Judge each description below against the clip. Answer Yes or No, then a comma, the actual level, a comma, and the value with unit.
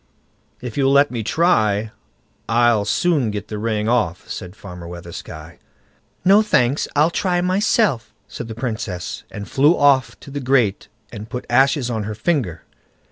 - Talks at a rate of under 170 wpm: Yes, average, 155 wpm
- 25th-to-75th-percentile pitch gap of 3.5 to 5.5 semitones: Yes, average, 5.2 semitones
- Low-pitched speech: Yes, low, 120 Hz